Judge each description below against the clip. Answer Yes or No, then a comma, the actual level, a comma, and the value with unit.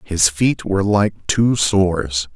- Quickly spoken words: No, average, 155 wpm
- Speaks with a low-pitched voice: Yes, very low, 95 Hz